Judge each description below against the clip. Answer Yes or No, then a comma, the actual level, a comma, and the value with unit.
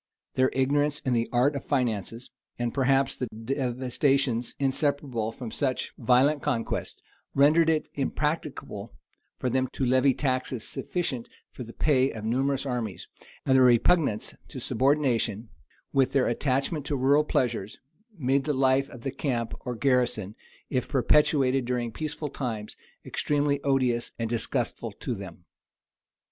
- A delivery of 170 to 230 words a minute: No, average, 140 wpm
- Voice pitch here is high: No, low, 130 Hz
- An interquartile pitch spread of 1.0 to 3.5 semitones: Yes, average, 2.9 semitones